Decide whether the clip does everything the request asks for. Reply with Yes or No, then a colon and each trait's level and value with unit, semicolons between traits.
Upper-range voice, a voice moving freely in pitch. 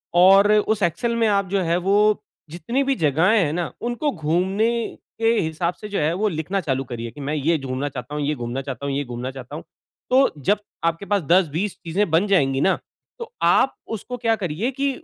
No: medium, 175 Hz; wide, 6.1 semitones